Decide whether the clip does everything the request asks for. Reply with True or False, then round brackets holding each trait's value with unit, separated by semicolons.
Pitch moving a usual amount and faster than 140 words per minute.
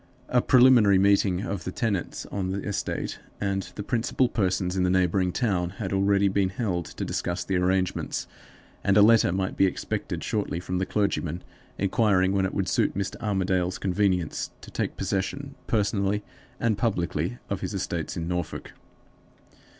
False (2.1 semitones; 165 wpm)